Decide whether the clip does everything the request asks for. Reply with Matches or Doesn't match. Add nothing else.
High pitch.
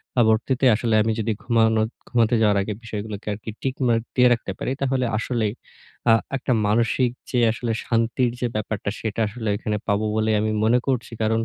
Doesn't match